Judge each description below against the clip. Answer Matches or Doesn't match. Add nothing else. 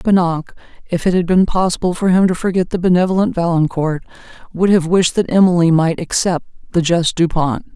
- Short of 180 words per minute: Doesn't match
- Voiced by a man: Doesn't match